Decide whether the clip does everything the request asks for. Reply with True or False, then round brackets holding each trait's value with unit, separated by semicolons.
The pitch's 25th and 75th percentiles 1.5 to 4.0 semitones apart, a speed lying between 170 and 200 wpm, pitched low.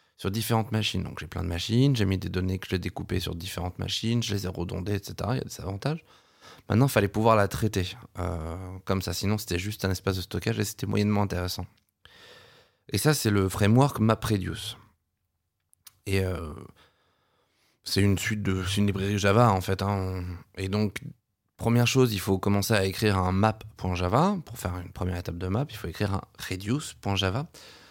True (3.1 semitones; 195 wpm; 100 Hz)